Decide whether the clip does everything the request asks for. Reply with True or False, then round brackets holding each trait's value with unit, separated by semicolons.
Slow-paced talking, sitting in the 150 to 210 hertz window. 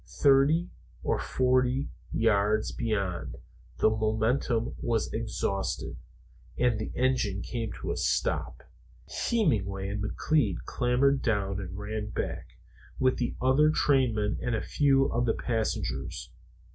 False (120 wpm; 115 Hz)